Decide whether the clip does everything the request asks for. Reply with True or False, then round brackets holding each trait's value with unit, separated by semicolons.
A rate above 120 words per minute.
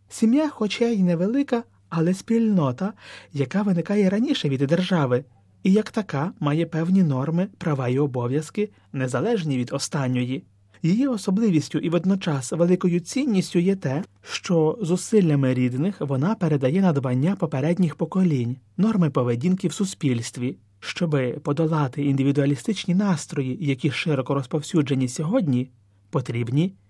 False (115 wpm)